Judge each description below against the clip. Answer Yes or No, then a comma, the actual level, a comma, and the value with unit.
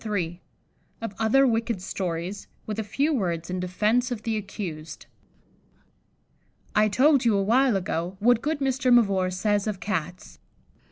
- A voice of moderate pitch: No, high, 210 Hz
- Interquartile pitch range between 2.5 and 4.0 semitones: No, average, 4.7 semitones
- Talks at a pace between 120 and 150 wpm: Yes, average, 145 wpm